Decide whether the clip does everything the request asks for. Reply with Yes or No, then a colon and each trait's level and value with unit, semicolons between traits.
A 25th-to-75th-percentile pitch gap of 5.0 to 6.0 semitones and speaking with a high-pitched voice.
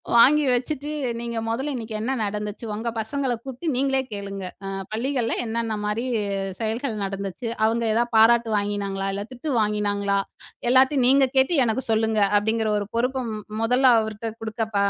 No: average, 3.4 semitones; high, 225 Hz